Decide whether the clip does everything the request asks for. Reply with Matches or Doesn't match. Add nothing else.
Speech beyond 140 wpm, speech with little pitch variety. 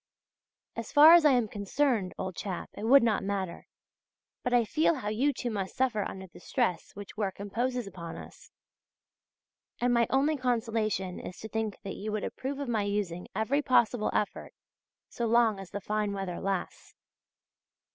Doesn't match